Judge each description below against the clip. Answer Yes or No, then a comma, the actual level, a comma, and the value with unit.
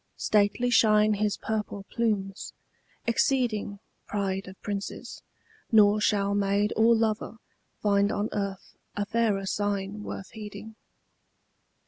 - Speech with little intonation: Yes, narrow, 1.4 semitones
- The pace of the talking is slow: Yes, slow, 110 wpm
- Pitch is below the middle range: No, high, 205 Hz